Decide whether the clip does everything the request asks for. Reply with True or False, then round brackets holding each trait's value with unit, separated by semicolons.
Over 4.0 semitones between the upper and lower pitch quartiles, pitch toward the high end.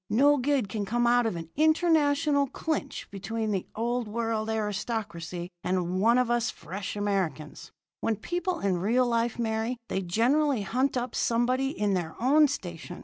True (4.5 semitones; 230 Hz)